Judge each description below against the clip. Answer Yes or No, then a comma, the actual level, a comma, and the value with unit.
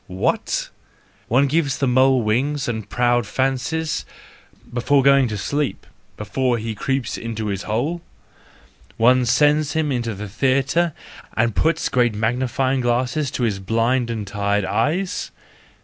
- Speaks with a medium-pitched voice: No, low, 125 Hz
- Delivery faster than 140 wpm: No, slow, 135 wpm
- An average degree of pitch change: Yes, average, 3.6 semitones